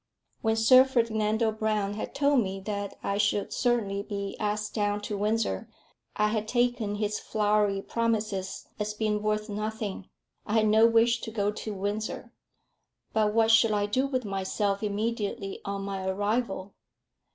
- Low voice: No, high, 210 Hz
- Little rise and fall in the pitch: Yes, narrow, 1.6 semitones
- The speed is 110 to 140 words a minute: No, average, 155 wpm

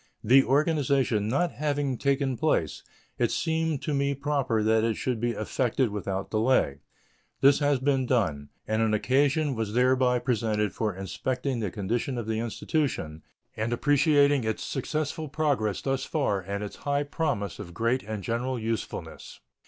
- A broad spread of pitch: No, average, 4.5 semitones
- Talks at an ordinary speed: Yes, average, 155 wpm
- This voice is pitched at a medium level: No, low, 125 Hz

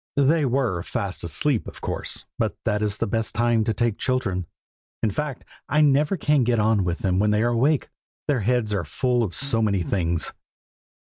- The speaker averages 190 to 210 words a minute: Yes, average, 195 wpm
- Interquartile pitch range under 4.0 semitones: No, average, 4.7 semitones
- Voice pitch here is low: Yes, low, 115 Hz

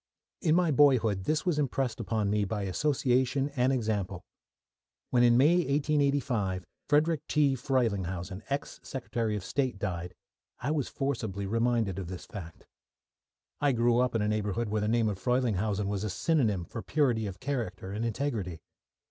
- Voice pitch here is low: Yes, low, 115 Hz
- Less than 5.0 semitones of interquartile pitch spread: No, average, 5.3 semitones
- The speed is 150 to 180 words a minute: Yes, average, 160 wpm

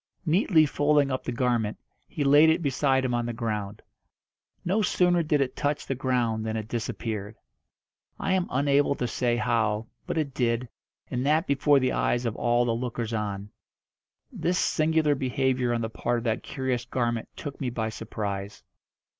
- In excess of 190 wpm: No, average, 175 wpm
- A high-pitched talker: No, low, 125 Hz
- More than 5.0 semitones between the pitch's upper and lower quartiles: No, average, 3.8 semitones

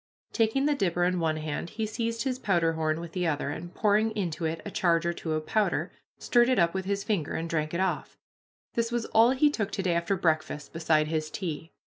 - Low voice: No, medium, 175 Hz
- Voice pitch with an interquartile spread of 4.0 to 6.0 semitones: Yes, average, 5.2 semitones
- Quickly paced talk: Yes, fast, 225 wpm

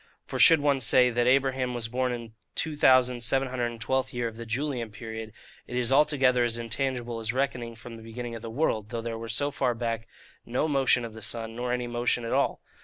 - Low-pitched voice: Yes, low, 120 Hz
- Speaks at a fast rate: Yes, fast, 235 wpm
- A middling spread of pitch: No, narrow, 2.1 semitones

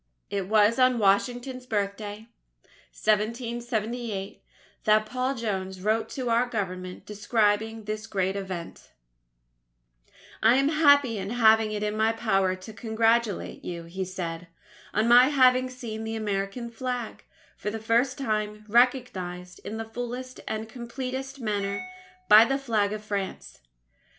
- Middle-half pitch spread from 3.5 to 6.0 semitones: No, average, 3.1 semitones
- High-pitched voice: Yes, high, 220 Hz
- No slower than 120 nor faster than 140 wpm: Yes, slow, 135 wpm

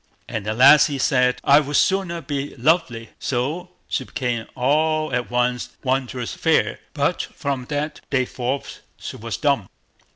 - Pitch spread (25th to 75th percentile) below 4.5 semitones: Yes, average, 3.5 semitones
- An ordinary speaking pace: Yes, average, 150 wpm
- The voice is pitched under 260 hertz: Yes, low, 135 Hz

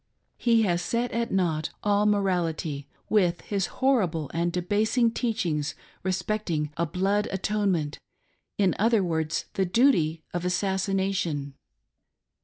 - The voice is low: No, high, 190 Hz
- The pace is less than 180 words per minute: Yes, slow, 135 wpm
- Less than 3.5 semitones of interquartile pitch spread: No, average, 4.0 semitones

